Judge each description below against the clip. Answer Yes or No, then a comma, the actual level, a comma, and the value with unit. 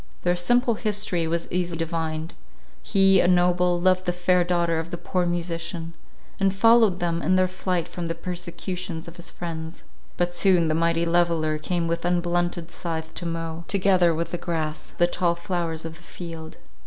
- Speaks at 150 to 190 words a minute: Yes, average, 180 wpm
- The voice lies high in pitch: No, medium, 175 Hz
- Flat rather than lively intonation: Yes, narrow, 1.5 semitones